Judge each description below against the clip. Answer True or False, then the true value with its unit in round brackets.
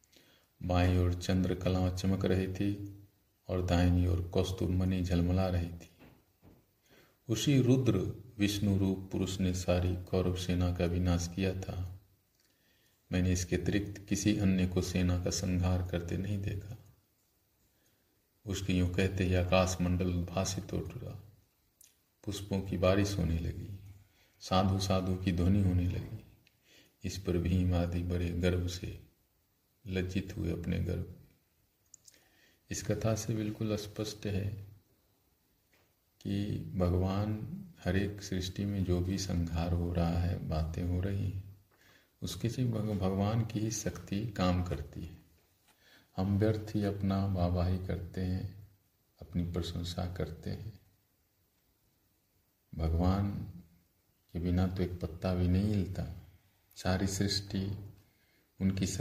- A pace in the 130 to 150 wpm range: False (120 wpm)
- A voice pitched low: True (95 Hz)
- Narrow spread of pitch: True (2.1 semitones)